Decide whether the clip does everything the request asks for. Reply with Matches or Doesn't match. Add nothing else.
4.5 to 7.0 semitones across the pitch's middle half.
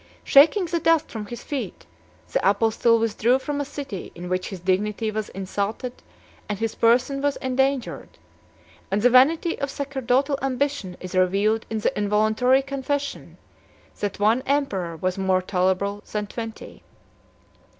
Matches